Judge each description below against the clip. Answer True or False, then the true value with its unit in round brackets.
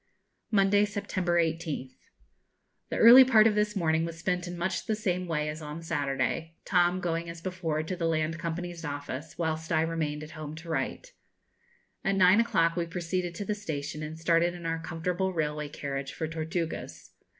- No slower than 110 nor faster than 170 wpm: False (180 wpm)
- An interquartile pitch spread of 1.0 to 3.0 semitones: True (2.5 semitones)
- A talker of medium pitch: True (165 Hz)